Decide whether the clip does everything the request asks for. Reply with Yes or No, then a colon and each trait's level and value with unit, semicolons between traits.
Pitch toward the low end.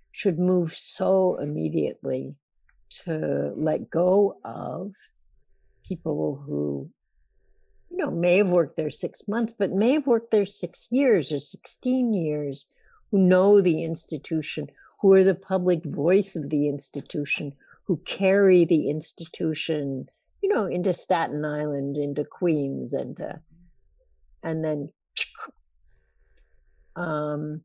No: medium, 160 Hz